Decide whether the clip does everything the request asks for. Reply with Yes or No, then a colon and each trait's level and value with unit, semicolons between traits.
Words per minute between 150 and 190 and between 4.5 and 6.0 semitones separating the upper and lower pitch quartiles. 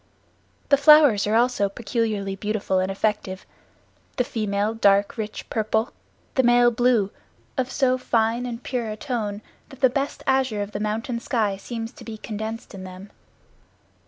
No: average, 160 wpm; average, 3.2 semitones